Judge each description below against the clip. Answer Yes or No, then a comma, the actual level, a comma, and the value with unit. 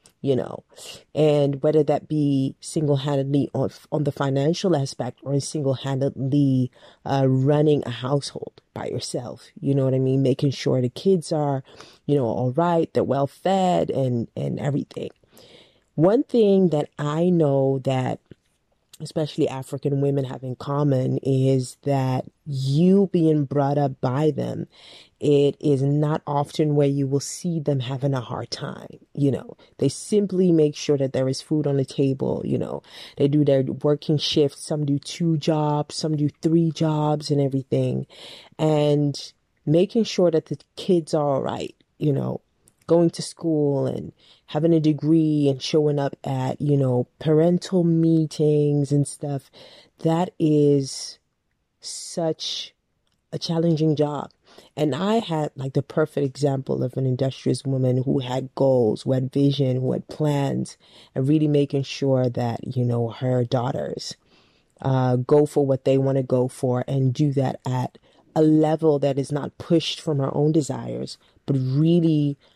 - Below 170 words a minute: Yes, average, 160 wpm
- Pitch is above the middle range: No, medium, 145 Hz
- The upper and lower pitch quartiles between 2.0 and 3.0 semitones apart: Yes, narrow, 2.6 semitones